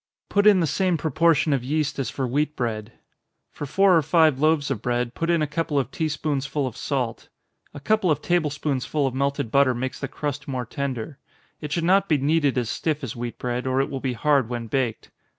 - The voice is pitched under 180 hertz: Yes, medium, 140 Hz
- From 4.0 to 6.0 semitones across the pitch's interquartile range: No, average, 3.5 semitones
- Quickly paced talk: Yes, fast, 220 wpm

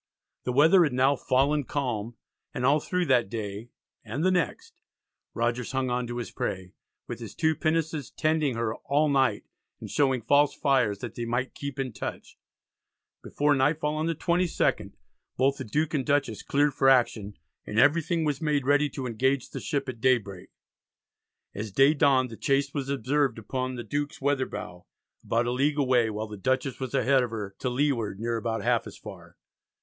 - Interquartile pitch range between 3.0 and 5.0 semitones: Yes, average, 3.6 semitones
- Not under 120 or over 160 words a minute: No, average, 185 wpm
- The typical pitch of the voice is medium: No, low, 130 Hz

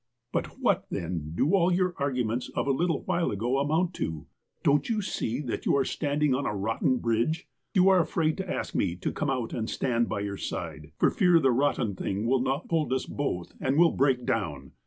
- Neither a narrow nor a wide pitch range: No, wide, 6.2 semitones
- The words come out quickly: Yes, fast, 220 wpm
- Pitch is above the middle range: No, low, 130 Hz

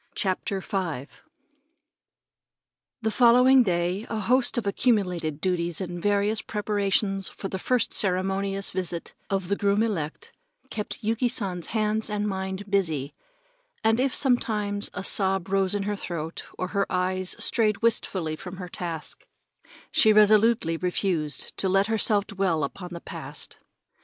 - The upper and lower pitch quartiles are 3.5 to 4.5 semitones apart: No, average, 2.9 semitones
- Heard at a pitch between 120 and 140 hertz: No, high, 195 Hz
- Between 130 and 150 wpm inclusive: Yes, average, 140 wpm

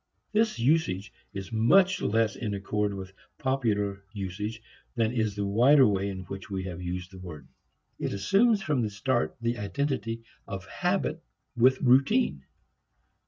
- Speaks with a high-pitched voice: No, low, 105 Hz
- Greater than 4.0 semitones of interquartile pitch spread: Yes, average, 5.1 semitones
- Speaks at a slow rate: No, average, 150 wpm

